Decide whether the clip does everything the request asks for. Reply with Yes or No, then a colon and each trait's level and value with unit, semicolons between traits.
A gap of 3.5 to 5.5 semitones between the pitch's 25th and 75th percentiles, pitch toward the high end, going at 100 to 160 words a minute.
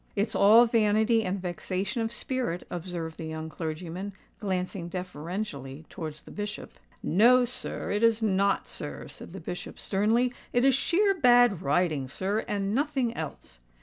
Yes: average, 5.0 semitones; high, 200 Hz; average, 145 wpm